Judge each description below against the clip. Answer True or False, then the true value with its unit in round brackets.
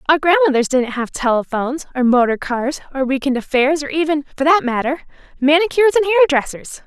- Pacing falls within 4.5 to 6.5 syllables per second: True (5.8 syllables/s)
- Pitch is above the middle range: True (285 Hz)